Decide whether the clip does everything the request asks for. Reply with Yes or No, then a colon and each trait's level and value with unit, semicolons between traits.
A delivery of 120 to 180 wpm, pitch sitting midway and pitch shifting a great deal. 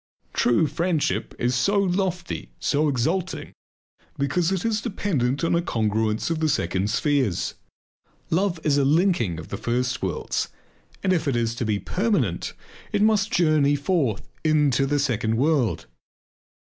Yes: average, 150 wpm; medium, 145 Hz; wide, 7.0 semitones